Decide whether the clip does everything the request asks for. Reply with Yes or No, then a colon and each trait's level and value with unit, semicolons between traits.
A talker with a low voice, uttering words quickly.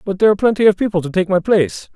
No: medium, 185 Hz; fast, 305 wpm